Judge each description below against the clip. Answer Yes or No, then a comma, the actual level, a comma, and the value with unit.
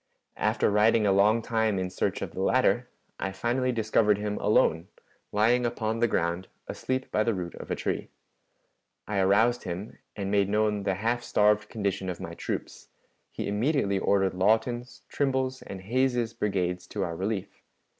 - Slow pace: No, average, 165 wpm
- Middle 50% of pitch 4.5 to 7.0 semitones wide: No, average, 3.3 semitones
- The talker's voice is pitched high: No, low, 105 Hz